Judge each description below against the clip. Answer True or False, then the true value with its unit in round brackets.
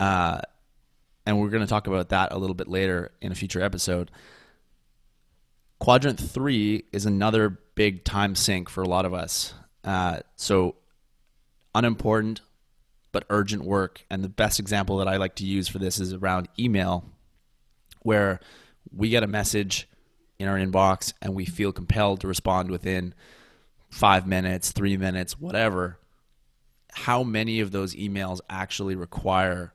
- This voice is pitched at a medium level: False (95 Hz)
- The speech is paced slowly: False (150 wpm)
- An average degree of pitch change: False (2.3 semitones)